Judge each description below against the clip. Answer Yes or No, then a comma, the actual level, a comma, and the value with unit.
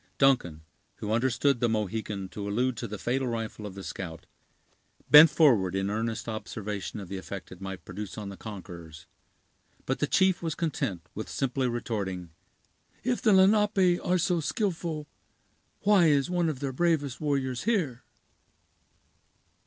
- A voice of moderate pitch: No, low, 120 Hz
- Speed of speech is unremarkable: Yes, average, 155 wpm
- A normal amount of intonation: No, wide, 7.8 semitones